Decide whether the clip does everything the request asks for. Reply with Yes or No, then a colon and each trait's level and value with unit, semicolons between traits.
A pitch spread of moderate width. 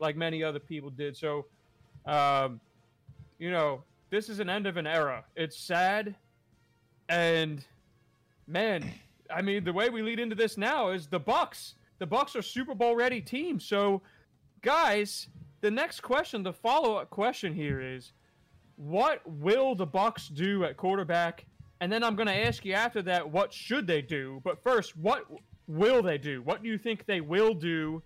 No: wide, 6.3 semitones